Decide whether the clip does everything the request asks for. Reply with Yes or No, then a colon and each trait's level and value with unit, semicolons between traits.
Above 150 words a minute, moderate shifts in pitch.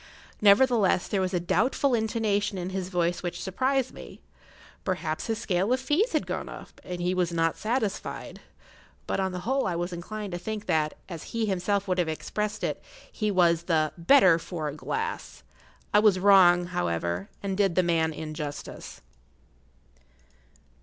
Yes: average, 165 wpm; average, 3.8 semitones